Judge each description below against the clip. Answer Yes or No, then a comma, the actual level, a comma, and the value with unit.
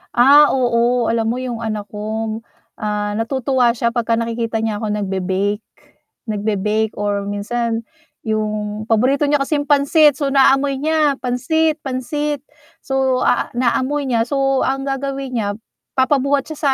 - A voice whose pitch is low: No, high, 245 Hz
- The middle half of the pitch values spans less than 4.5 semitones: Yes, average, 4.0 semitones